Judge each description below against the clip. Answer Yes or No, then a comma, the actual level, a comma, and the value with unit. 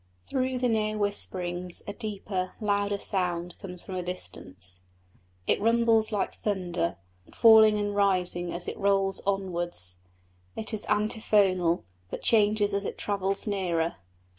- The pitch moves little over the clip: No, average, 3.0 semitones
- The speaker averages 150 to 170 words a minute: No, slow, 135 wpm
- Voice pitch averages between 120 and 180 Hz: No, high, 195 Hz